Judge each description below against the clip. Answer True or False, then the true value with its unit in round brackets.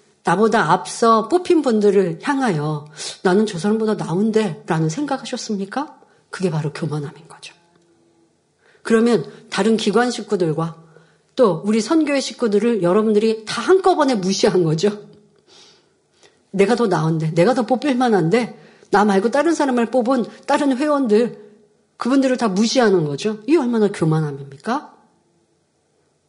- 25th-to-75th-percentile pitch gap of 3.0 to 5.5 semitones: True (5.2 semitones)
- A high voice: True (215 Hz)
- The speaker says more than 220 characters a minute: True (295 characters per minute)